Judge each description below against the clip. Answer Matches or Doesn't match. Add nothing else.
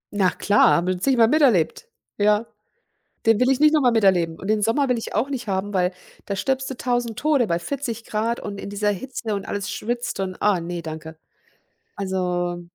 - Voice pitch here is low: Doesn't match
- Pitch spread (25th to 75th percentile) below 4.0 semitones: Doesn't match